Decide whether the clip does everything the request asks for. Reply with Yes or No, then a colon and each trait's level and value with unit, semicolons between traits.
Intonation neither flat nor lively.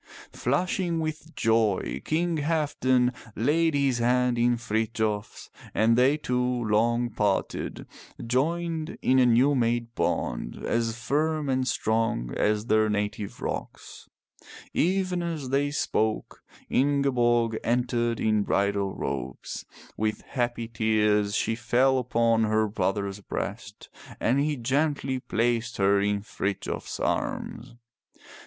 Yes: average, 4.1 semitones